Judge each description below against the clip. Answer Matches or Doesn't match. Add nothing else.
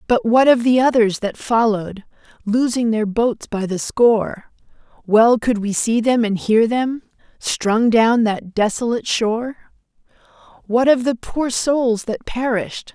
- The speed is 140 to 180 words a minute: Matches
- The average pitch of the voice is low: Doesn't match